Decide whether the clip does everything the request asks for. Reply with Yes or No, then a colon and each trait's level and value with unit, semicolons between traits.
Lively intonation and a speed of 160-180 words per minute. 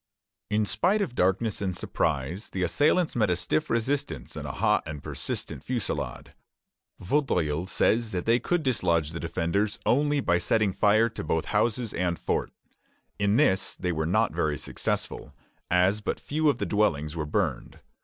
Yes: wide, 5.7 semitones; average, 165 wpm